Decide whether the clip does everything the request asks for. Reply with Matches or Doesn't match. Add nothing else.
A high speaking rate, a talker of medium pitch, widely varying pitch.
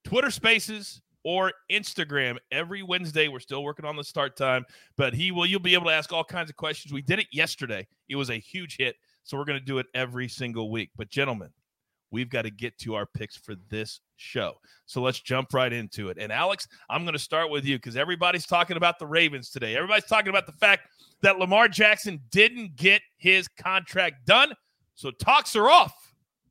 Matches